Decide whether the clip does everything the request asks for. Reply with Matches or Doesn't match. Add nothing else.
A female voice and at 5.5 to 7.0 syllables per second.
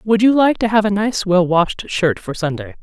Doesn't match